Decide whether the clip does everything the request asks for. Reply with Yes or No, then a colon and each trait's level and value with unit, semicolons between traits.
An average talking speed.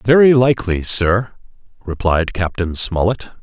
No: slow, 105 wpm